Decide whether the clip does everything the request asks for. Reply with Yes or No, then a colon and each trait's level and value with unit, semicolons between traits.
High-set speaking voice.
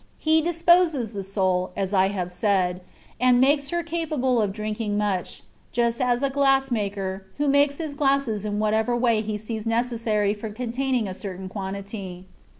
Yes: high, 220 Hz